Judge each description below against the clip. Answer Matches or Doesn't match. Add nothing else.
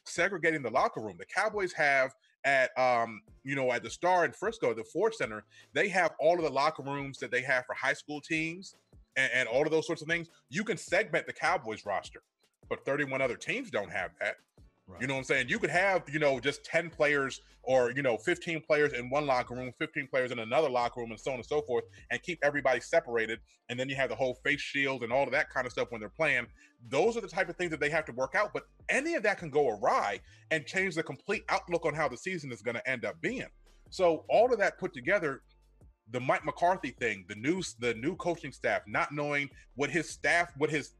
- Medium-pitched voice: Matches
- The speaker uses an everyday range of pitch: Matches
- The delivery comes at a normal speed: Doesn't match